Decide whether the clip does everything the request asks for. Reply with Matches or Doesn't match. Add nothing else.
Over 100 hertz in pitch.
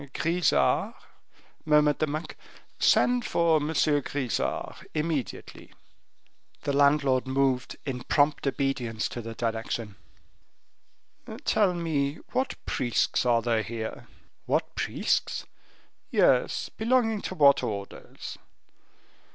Matches